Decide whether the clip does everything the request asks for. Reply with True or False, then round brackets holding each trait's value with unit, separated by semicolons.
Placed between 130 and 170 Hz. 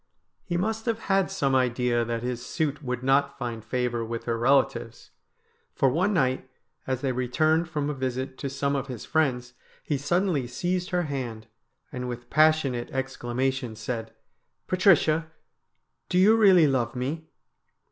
True (135 Hz)